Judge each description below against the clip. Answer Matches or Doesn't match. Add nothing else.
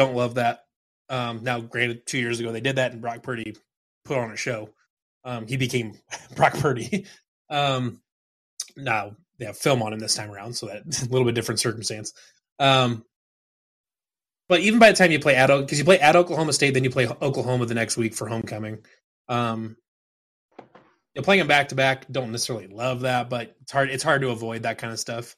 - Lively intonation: Doesn't match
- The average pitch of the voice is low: Matches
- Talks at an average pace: Doesn't match